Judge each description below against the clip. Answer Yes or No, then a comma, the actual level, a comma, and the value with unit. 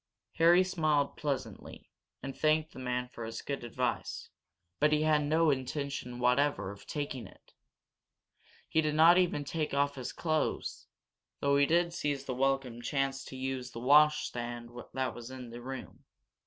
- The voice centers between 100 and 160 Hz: Yes, medium, 140 Hz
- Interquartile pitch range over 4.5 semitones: No, average, 3.4 semitones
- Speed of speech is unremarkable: Yes, average, 160 wpm